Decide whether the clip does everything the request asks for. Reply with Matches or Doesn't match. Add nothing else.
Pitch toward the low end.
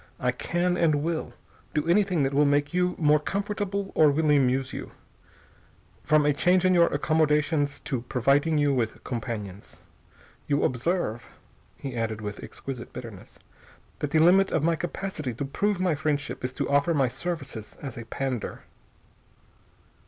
Doesn't match